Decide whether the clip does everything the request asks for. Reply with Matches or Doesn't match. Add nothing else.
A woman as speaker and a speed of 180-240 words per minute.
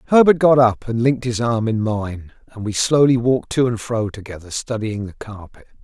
Doesn't match